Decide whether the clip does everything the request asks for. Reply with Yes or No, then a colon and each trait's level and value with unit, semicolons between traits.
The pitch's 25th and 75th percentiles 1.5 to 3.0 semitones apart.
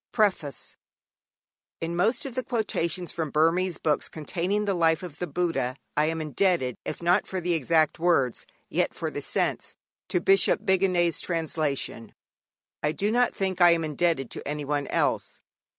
No: average, 3.4 semitones